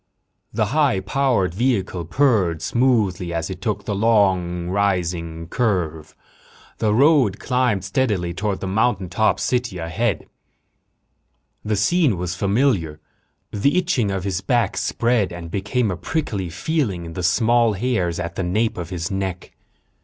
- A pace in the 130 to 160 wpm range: Yes, average, 140 wpm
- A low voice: Yes, low, 100 Hz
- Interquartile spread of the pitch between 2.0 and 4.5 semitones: No, average, 5.1 semitones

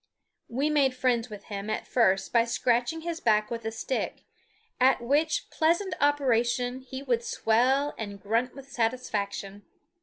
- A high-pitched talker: Yes, high, 245 Hz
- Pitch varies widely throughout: No, average, 3.5 semitones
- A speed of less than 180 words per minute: Yes, average, 150 wpm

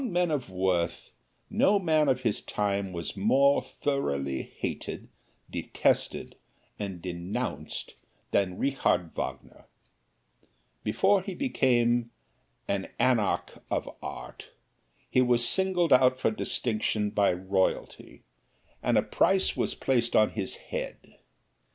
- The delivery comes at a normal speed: No, slow, 115 wpm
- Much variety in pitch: Yes, wide, 6.4 semitones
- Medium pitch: No, low, 120 Hz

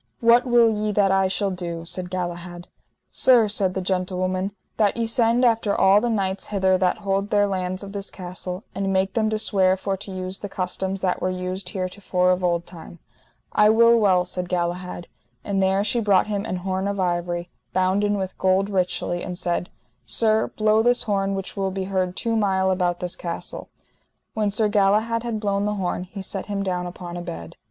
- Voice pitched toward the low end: No, high, 190 Hz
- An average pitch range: No, narrow, 2.2 semitones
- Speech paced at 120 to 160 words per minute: No, average, 200 wpm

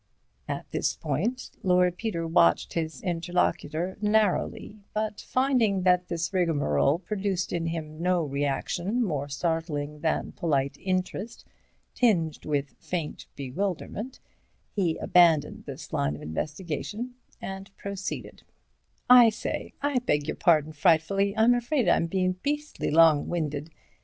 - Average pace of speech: No, slow, 120 wpm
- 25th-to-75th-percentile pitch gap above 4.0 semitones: Yes, average, 4.6 semitones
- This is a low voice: No, medium, 175 Hz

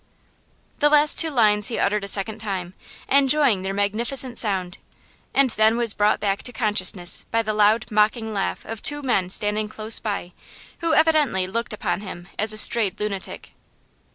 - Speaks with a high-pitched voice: Yes, high, 215 Hz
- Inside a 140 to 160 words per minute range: No, average, 170 wpm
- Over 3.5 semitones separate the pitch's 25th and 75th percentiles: No, average, 3.1 semitones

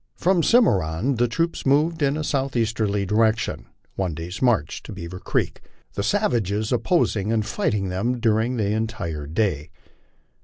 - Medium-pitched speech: No, low, 110 Hz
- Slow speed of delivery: No, average, 150 wpm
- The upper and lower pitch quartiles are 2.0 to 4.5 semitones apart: No, average, 4.9 semitones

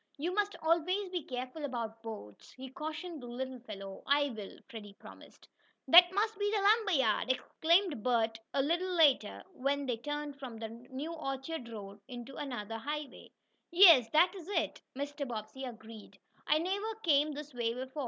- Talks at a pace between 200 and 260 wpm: No, average, 170 wpm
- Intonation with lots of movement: Yes, wide, 6.0 semitones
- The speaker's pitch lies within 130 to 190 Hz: No, very high, 275 Hz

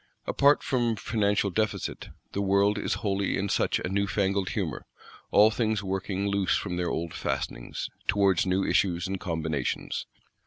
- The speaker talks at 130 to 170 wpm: Yes, average, 155 wpm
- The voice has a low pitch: Yes, low, 100 Hz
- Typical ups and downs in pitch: No, narrow, 1.8 semitones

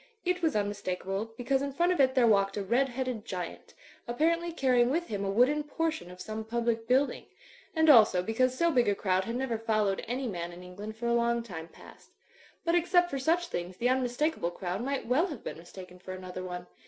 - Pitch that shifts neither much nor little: No, wide, 5.8 semitones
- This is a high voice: Yes, high, 235 Hz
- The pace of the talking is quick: Yes, fast, 215 wpm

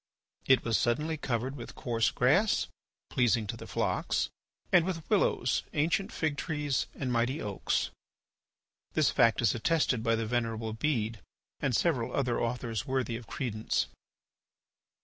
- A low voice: Yes, low, 125 Hz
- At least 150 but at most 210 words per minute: No, slow, 135 wpm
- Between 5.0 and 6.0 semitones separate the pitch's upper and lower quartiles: No, average, 4.1 semitones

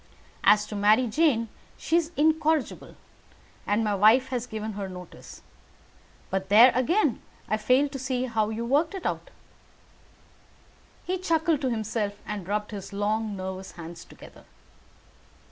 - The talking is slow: No, average, 145 wpm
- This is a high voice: Yes, high, 225 Hz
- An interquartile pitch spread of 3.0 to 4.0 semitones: No, average, 5.1 semitones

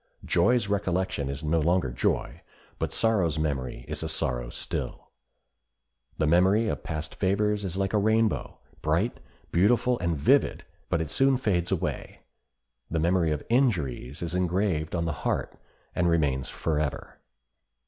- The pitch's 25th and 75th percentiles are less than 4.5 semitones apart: No, average, 4.9 semitones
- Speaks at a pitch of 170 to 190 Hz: No, very low, 85 Hz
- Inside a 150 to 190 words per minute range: No, average, 140 wpm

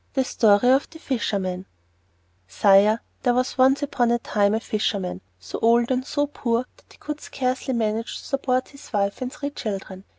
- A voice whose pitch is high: Yes, high, 235 Hz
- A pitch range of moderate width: Yes, average, 4.3 semitones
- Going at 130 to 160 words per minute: No, average, 185 wpm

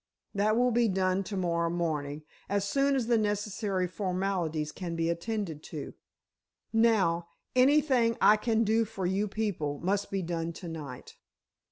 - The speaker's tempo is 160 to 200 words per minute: No, average, 150 wpm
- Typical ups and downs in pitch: Yes, average, 4.6 semitones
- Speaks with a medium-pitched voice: No, high, 195 Hz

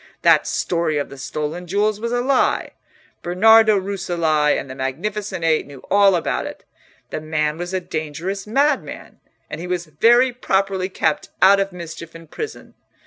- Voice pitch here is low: No, medium, 180 Hz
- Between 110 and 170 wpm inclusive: Yes, average, 165 wpm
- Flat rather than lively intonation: No, average, 4.5 semitones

